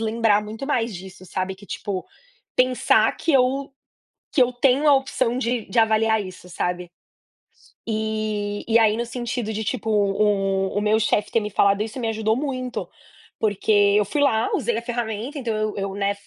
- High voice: Yes, high, 220 Hz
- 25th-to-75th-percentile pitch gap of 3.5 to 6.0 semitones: No, average, 2.9 semitones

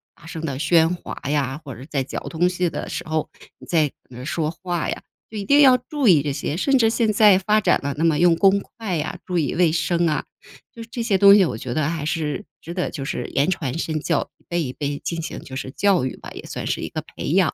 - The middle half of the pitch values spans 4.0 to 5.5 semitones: Yes, average, 4.7 semitones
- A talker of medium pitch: Yes, medium, 165 Hz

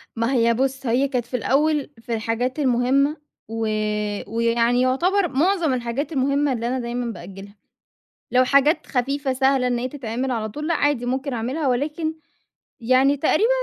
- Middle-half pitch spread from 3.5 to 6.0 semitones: No, average, 3.1 semitones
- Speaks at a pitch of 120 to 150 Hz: No, very high, 255 Hz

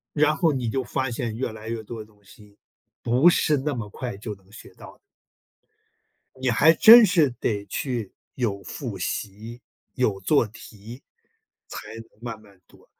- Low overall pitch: Yes, low, 115 Hz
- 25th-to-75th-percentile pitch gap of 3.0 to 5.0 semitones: Yes, average, 3.9 semitones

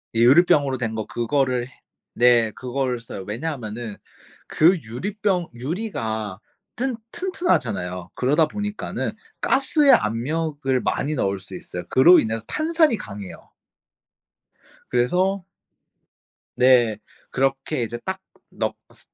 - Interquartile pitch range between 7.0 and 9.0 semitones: Yes, wide, 7.8 semitones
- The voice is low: Yes, low, 130 Hz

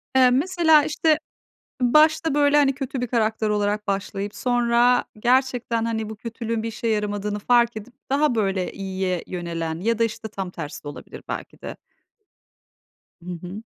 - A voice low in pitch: No, high, 225 Hz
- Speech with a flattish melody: No, average, 3.8 semitones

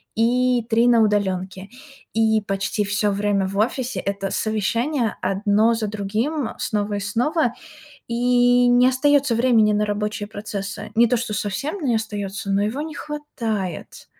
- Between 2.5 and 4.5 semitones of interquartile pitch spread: Yes, average, 3.2 semitones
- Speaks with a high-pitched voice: Yes, high, 220 Hz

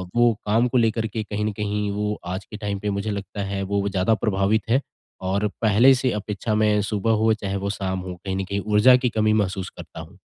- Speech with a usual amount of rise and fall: No, narrow, 1.9 semitones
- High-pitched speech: No, low, 105 Hz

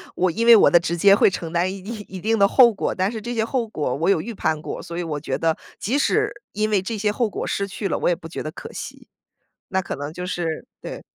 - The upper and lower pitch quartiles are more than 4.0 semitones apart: Yes, average, 4.4 semitones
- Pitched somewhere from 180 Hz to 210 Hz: Yes, high, 190 Hz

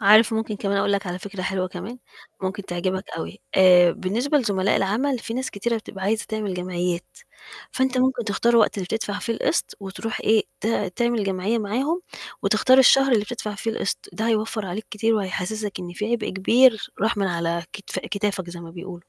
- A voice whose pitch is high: Yes, high, 205 Hz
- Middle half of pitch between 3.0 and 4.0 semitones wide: Yes, average, 3.4 semitones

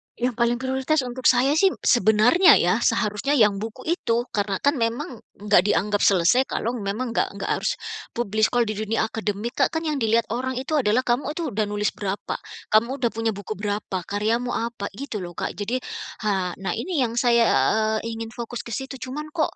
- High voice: Yes, high, 230 Hz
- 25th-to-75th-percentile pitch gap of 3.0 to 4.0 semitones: Yes, average, 3.6 semitones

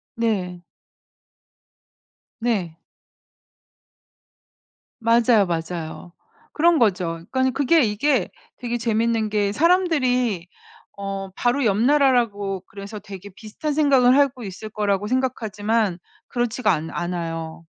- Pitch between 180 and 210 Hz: No, high, 220 Hz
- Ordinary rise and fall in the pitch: Yes, average, 4.5 semitones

